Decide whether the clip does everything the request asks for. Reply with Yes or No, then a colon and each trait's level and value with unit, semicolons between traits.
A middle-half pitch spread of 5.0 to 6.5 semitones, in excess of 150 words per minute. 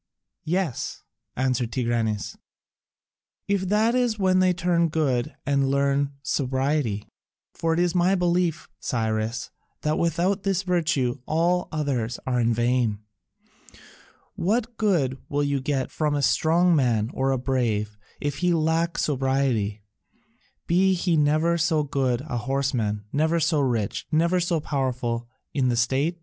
No: wide, 5.4 semitones; average, 140 wpm